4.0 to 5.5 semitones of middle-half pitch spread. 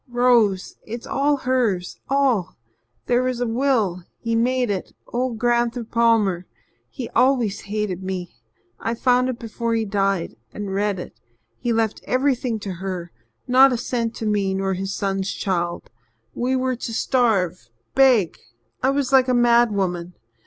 Yes: average, 4.4 semitones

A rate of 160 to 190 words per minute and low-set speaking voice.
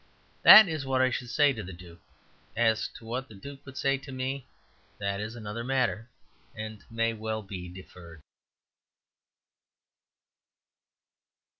No: average, 140 wpm; low, 115 Hz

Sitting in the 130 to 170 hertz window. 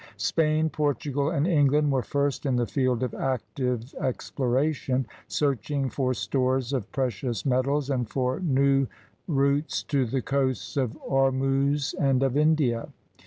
Yes: low, 135 Hz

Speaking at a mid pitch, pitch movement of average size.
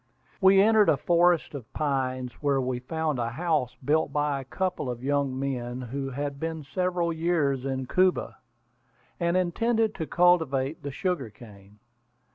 Yes: medium, 145 Hz; average, 5.0 semitones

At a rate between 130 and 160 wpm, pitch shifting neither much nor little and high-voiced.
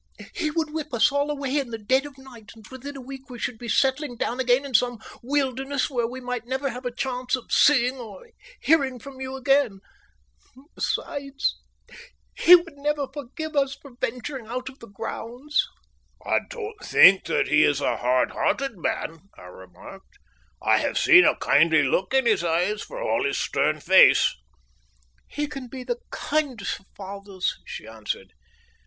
No: average, 180 wpm; average, 4.5 semitones; very high, 255 Hz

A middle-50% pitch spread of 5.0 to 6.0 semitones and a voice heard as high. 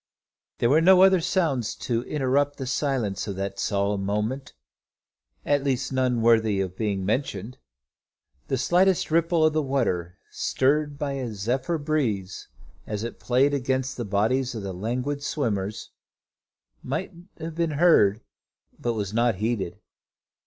No: wide, 5.5 semitones; low, 125 Hz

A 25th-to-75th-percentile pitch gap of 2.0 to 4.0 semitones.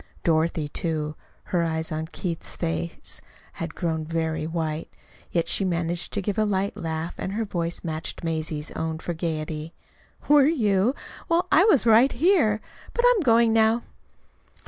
No: wide, 5.5 semitones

